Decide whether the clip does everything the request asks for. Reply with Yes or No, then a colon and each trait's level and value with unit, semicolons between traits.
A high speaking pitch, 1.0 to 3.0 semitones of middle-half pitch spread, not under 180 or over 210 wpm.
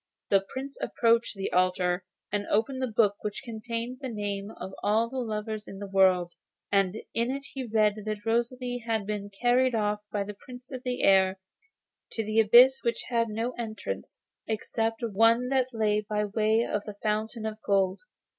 Yes: high, 220 Hz; narrow, 2.6 semitones; average, 185 wpm